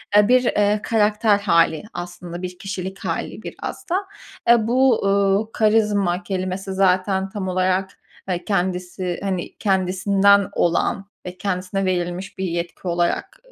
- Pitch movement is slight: Yes, narrow, 2.2 semitones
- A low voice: No, high, 190 Hz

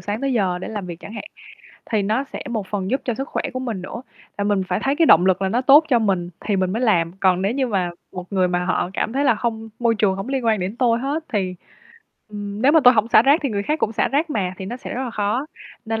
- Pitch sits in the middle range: No, high, 215 Hz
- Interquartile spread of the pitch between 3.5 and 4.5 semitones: No, average, 4.9 semitones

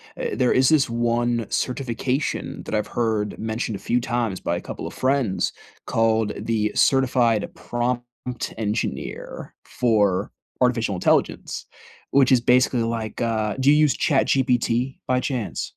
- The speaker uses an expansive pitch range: No, narrow, 2.5 semitones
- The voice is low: Yes, low, 120 Hz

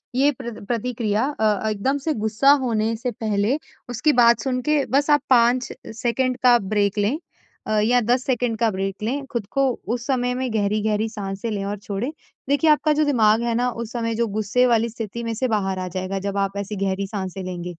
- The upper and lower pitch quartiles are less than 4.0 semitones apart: Yes, average, 3.4 semitones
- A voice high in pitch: Yes, high, 225 Hz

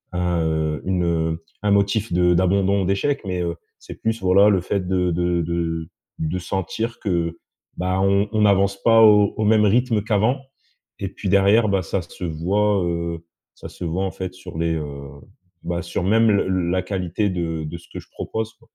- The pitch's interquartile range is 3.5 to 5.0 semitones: No, average, 3.1 semitones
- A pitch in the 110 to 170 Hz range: No, very low, 95 Hz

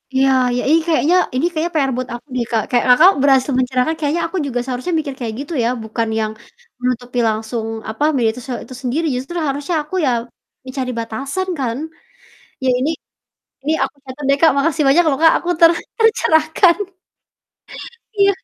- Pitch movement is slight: No, average, 4.2 semitones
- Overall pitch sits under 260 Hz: No, very high, 270 Hz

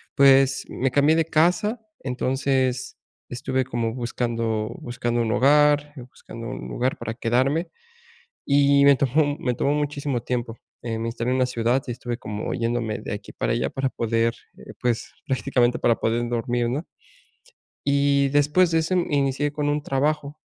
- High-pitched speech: No, low, 130 Hz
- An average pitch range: Yes, average, 3.2 semitones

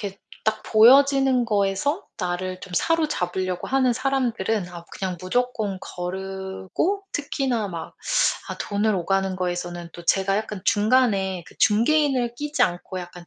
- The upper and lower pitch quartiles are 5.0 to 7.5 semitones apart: Yes, wide, 5.4 semitones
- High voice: Yes, high, 200 Hz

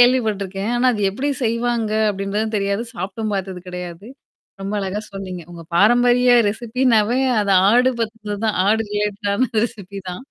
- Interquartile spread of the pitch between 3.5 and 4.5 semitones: No, average, 3.1 semitones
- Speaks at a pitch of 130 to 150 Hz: No, high, 210 Hz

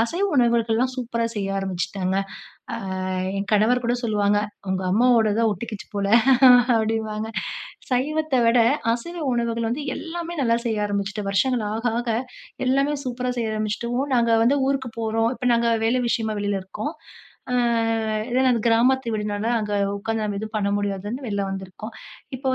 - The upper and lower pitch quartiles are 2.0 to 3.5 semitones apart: Yes, average, 3.1 semitones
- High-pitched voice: Yes, high, 225 Hz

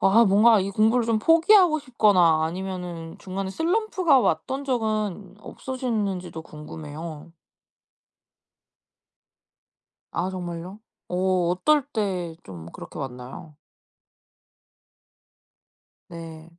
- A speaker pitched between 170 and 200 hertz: Yes, high, 190 Hz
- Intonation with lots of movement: Yes, wide, 5.9 semitones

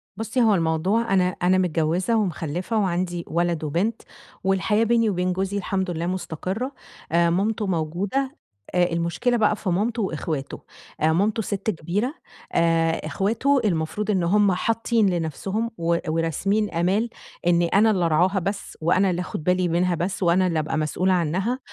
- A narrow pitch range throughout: No, average, 3.7 semitones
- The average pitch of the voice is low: No, medium, 185 Hz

